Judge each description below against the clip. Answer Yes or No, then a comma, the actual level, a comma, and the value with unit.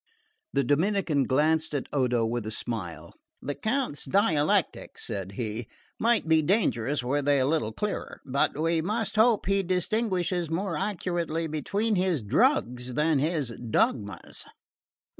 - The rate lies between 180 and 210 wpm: No, average, 140 wpm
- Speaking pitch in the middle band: Yes, medium, 155 Hz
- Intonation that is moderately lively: No, wide, 6.8 semitones